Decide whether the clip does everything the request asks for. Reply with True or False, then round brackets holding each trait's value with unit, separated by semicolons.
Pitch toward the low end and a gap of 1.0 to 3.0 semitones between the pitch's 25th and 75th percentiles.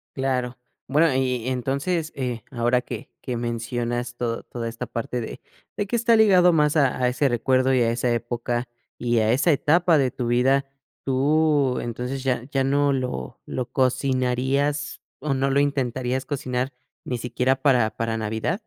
True (130 Hz; 2.6 semitones)